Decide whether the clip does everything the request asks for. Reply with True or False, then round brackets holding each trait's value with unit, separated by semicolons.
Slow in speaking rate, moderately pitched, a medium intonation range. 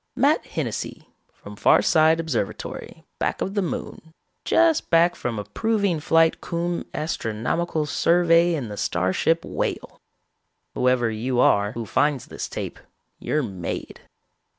False (130 wpm; 155 Hz; 7.0 semitones)